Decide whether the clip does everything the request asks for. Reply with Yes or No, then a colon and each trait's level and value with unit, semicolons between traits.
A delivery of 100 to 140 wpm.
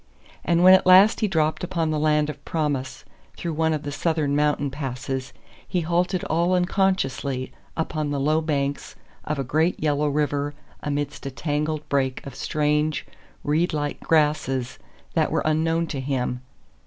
No: average, 160 wpm